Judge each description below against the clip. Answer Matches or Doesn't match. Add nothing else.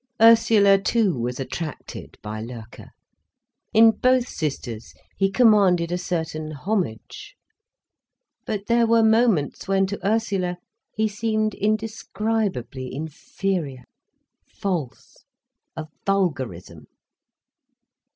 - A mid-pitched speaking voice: Doesn't match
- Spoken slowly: Matches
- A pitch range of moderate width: Doesn't match